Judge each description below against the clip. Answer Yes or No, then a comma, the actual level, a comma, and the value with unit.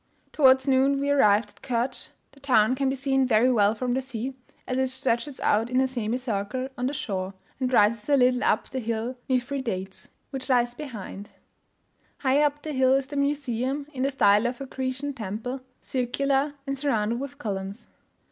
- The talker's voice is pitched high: Yes, very high, 255 Hz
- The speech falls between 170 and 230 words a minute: Yes, average, 185 wpm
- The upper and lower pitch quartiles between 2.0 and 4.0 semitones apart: Yes, average, 2.9 semitones